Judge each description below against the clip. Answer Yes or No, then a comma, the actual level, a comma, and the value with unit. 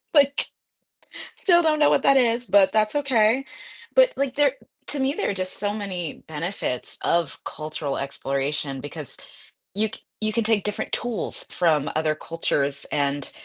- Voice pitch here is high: Yes, high, 200 Hz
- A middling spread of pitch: No, wide, 8.6 semitones